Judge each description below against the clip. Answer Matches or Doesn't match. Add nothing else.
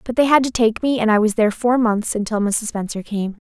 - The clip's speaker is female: Matches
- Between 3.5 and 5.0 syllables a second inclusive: Doesn't match